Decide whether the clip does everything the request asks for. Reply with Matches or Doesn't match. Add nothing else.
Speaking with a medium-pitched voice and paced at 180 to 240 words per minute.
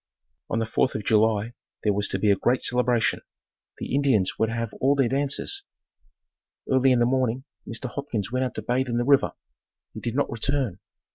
Doesn't match